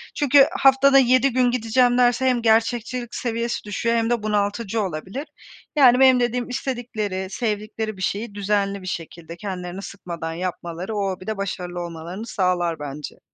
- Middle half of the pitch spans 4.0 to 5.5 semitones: Yes, average, 4.7 semitones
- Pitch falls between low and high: No, high, 215 Hz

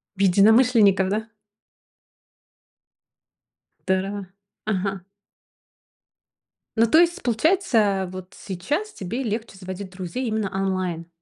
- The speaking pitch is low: No, high, 200 Hz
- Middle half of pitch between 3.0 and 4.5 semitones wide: Yes, average, 3.5 semitones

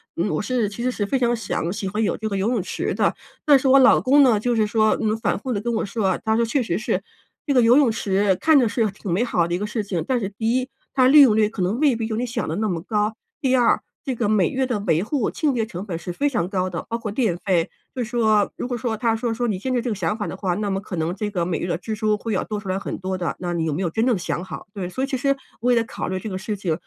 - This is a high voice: Yes, high, 215 Hz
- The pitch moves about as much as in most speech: Yes, average, 4.0 semitones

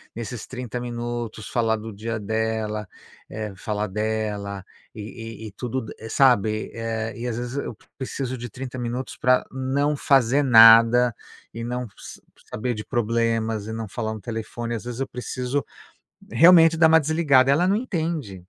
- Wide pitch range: No, average, 2.8 semitones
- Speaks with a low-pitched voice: Yes, low, 120 Hz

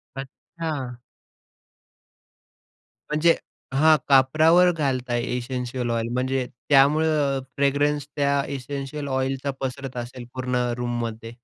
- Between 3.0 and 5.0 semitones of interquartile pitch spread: No, narrow, 2.6 semitones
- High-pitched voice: No, low, 135 Hz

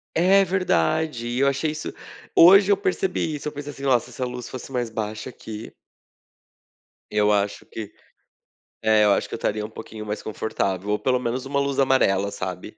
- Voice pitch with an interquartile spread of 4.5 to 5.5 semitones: Yes, average, 5.2 semitones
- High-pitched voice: No, low, 120 Hz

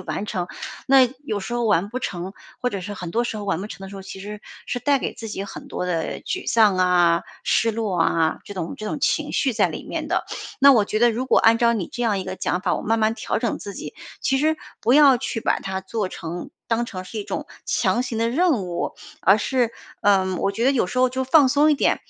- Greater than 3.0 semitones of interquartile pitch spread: Yes, average, 4.6 semitones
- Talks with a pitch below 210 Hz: No, high, 215 Hz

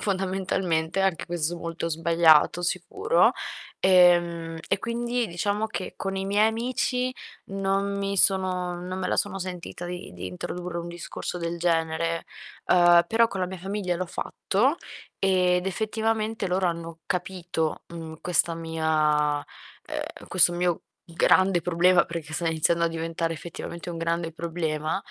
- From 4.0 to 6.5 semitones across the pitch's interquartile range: No, narrow, 2.6 semitones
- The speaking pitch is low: No, medium, 175 Hz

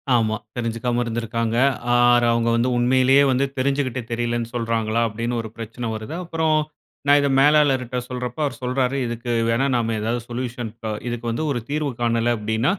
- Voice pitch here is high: No, low, 120 Hz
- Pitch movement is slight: Yes, narrow, 1.9 semitones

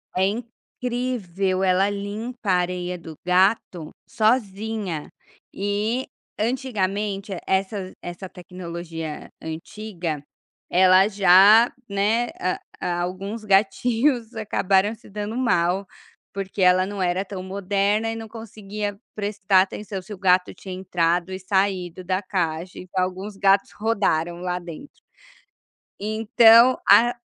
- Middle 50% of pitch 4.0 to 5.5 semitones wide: No, average, 2.8 semitones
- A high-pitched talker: Yes, high, 195 Hz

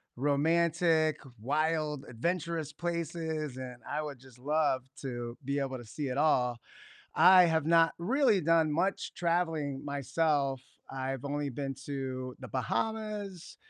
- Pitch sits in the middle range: Yes, medium, 150 Hz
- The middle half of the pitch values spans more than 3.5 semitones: Yes, average, 3.9 semitones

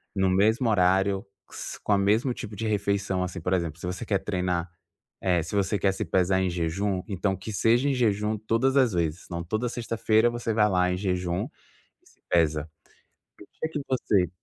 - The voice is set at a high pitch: No, low, 100 Hz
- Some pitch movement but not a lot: Yes, average, 3.4 semitones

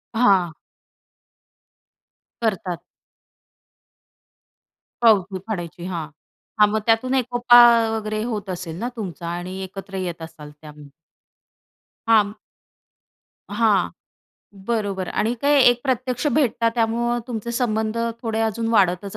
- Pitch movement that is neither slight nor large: Yes, average, 4.1 semitones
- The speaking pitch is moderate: No, high, 215 Hz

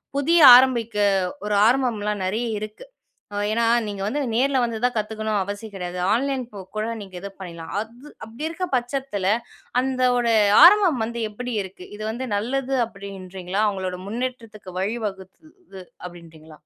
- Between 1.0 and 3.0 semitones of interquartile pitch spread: No, average, 4.5 semitones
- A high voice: Yes, high, 220 Hz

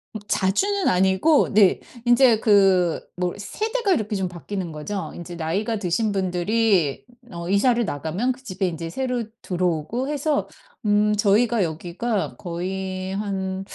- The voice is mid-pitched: No, high, 195 Hz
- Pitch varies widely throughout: No, average, 4.4 semitones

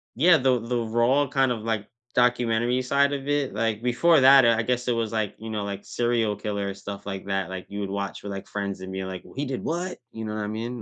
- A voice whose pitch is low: Yes, low, 115 Hz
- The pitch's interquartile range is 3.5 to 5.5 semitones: Yes, average, 3.9 semitones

